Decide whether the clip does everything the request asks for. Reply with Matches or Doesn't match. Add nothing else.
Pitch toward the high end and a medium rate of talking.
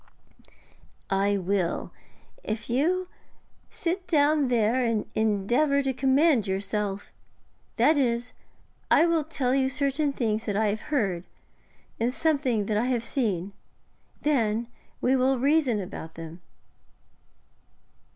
Doesn't match